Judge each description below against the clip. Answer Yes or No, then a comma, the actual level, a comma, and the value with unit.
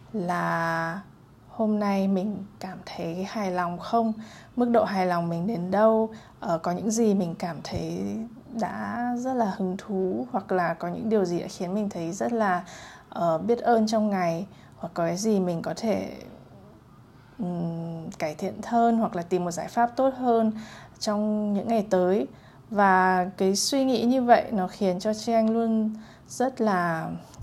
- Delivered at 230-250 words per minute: No, average, 175 wpm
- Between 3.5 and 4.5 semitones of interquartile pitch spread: Yes, average, 3.9 semitones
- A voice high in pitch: Yes, high, 200 Hz